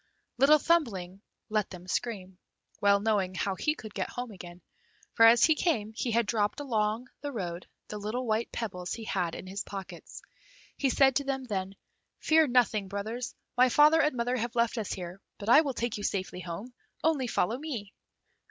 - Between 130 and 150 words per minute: No, average, 190 wpm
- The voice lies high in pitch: Yes, high, 220 Hz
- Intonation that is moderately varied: Yes, average, 4.5 semitones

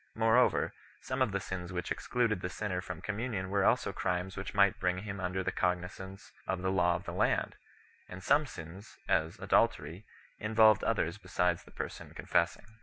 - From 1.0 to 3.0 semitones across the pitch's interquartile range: Yes, narrow, 2.5 semitones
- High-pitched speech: No, very low, 95 Hz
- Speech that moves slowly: No, average, 180 wpm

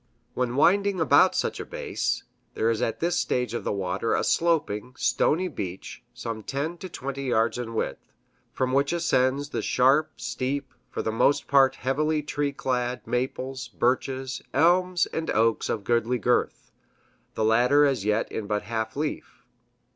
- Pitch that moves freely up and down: No, average, 3.8 semitones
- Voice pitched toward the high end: No, low, 130 Hz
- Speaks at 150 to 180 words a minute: Yes, average, 160 wpm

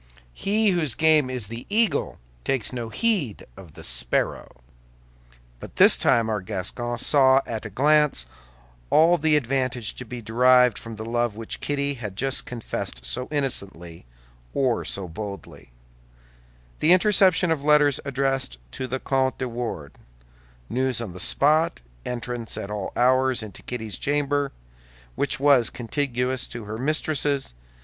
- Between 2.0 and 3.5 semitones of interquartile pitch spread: No, average, 4.4 semitones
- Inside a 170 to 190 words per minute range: No, average, 145 wpm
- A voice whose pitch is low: Yes, low, 125 Hz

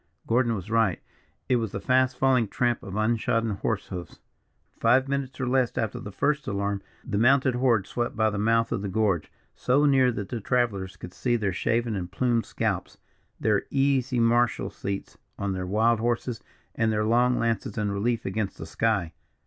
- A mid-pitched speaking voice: No, low, 115 Hz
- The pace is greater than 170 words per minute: Yes, average, 185 wpm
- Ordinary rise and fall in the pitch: Yes, average, 3.5 semitones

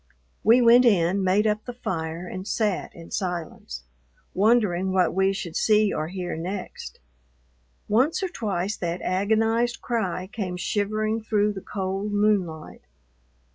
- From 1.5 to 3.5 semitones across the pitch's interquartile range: Yes, average, 3.2 semitones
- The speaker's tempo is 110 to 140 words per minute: Yes, slow, 135 wpm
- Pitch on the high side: Yes, high, 200 Hz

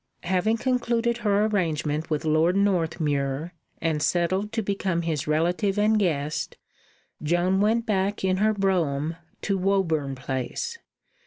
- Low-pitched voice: No, medium, 180 Hz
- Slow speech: Yes, slow, 130 wpm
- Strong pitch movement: No, average, 4.7 semitones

